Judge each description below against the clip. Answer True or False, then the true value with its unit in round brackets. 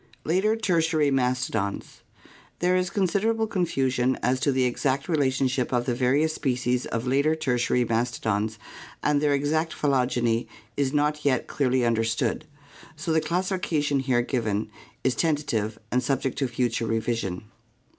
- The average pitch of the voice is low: True (130 Hz)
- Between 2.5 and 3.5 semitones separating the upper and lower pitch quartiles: False (4.1 semitones)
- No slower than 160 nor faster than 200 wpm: False (145 wpm)